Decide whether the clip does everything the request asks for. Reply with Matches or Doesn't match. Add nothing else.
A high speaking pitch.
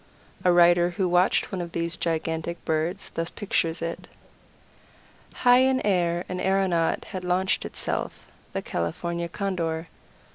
Doesn't match